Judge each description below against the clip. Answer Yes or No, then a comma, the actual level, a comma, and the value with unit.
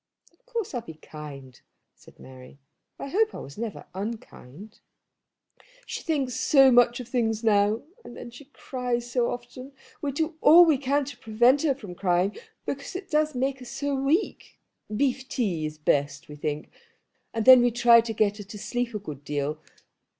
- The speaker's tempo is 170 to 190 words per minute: Yes, average, 180 wpm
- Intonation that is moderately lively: No, wide, 5.7 semitones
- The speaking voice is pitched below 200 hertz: No, high, 240 Hz